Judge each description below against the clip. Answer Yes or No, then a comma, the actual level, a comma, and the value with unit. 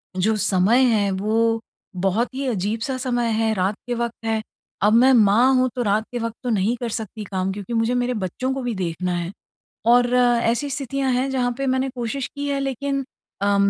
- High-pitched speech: Yes, high, 235 Hz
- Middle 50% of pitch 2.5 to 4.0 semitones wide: Yes, average, 3.7 semitones